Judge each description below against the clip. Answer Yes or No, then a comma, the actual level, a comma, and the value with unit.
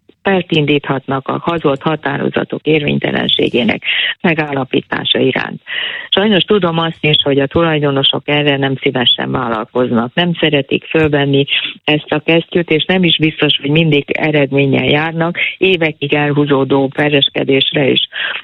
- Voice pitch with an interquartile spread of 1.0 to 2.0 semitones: No, average, 2.9 semitones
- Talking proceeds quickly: No, average, 115 wpm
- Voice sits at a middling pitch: Yes, medium, 150 Hz